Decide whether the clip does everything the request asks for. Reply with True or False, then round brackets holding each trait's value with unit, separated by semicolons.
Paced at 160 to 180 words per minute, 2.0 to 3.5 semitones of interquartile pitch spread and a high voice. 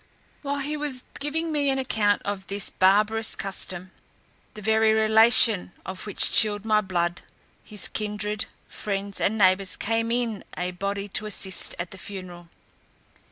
False (150 wpm; 2.6 semitones; 210 Hz)